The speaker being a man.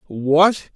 Yes: male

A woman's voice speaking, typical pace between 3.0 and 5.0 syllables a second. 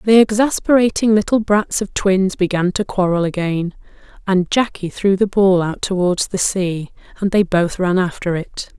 Yes: female; 4.6 syllables/s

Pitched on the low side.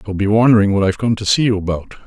Yes: low, 105 Hz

